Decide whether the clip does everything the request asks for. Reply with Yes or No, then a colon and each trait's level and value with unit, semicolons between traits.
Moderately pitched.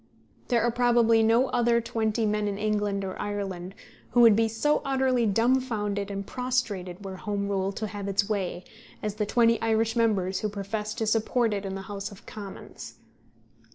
No: high, 215 Hz